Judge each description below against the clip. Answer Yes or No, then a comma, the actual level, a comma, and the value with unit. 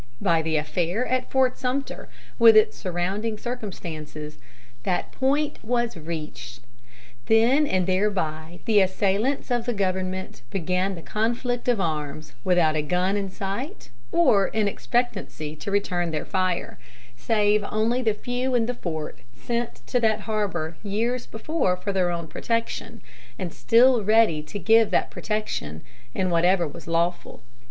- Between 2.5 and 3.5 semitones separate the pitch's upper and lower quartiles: No, average, 5.1 semitones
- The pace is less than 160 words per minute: Yes, average, 145 wpm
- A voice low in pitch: No, high, 200 Hz